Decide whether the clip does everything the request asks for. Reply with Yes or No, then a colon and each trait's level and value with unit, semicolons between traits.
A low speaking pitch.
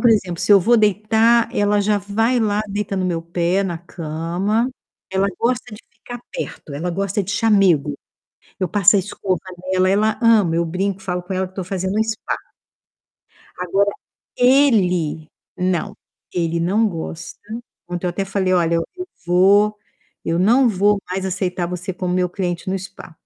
No: high, 190 Hz